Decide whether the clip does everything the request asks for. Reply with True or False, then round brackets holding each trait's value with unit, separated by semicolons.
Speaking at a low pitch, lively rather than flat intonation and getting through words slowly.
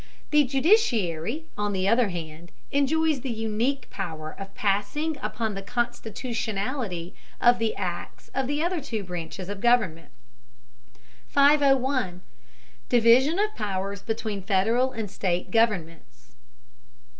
False (220 Hz; 5.7 semitones; 120 wpm)